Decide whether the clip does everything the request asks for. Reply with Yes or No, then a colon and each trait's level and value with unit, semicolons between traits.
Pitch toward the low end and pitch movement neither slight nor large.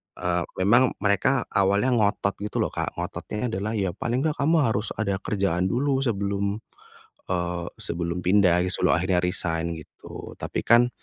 Yes: low, 100 Hz; average, 4.0 semitones